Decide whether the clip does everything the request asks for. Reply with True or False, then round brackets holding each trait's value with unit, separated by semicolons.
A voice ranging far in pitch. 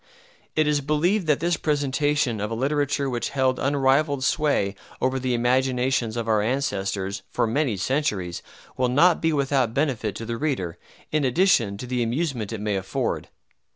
False (4.3 semitones)